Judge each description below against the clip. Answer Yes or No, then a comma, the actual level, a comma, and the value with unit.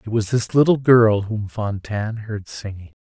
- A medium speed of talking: Yes, average, 180 wpm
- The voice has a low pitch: Yes, low, 110 Hz